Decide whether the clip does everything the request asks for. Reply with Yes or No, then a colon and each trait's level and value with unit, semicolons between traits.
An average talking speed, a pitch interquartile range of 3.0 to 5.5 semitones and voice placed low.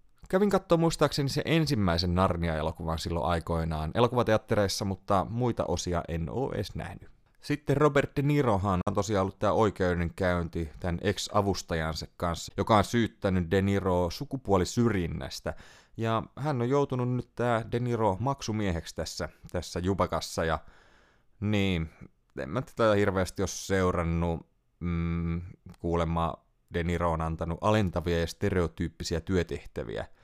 Yes: average, 125 wpm; average, 5.1 semitones; very low, 95 Hz